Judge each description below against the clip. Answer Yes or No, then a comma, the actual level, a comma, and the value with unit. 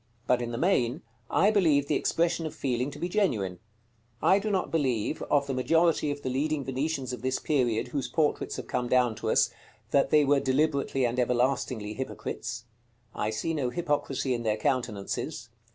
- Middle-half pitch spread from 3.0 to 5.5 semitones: Yes, average, 4.1 semitones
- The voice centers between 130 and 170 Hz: Yes, low, 135 Hz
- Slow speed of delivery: No, average, 185 wpm